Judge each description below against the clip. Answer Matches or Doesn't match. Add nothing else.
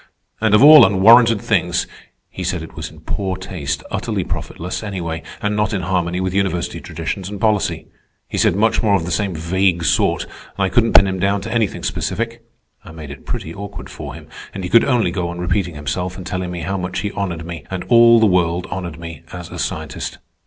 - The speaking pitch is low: Matches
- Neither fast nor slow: Doesn't match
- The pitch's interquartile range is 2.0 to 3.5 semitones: Matches